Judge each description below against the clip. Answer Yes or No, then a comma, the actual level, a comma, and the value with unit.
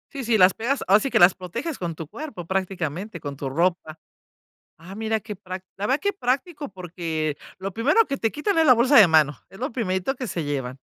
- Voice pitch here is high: Yes, high, 195 Hz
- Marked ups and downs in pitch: Yes, wide, 7.0 semitones